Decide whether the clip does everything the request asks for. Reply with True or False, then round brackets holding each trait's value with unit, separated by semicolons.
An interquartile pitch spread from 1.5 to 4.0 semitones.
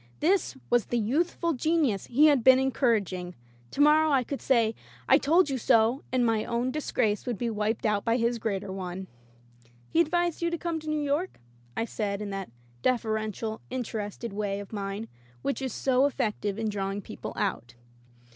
False (5.2 semitones)